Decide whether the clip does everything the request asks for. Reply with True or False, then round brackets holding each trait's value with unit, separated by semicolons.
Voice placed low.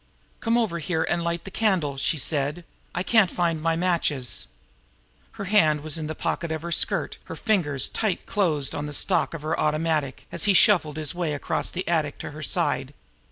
False (165 Hz)